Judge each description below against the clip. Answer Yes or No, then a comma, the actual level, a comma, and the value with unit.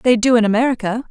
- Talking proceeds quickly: Yes, fast, 215 wpm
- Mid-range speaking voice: No, high, 235 Hz